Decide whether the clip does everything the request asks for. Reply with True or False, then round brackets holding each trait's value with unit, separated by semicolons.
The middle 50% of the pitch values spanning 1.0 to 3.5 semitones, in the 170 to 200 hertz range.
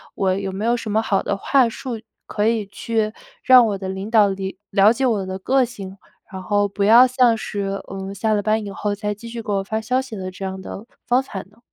False (2.9 semitones; 210 Hz)